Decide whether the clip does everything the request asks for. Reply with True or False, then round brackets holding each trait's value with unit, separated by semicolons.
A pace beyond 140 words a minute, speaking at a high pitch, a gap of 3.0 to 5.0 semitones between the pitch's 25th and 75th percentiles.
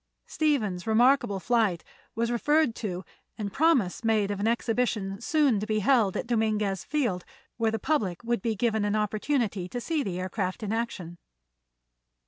True (160 wpm; 220 Hz; 3.4 semitones)